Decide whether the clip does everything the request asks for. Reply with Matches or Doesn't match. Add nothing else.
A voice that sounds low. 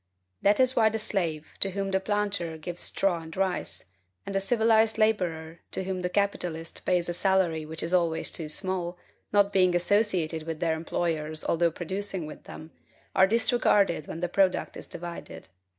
Doesn't match